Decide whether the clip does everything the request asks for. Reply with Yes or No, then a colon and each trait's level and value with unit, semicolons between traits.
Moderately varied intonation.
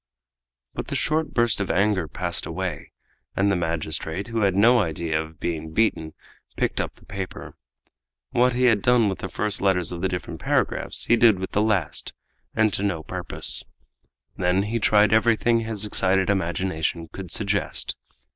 Yes: average, 3.9 semitones